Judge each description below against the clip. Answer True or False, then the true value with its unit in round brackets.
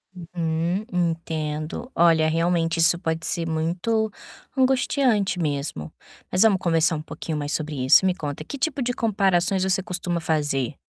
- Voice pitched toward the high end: False (170 Hz)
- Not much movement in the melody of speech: False (3.2 semitones)